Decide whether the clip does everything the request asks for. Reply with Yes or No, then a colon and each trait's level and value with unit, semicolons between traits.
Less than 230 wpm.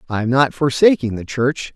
Yes: fast, 205 wpm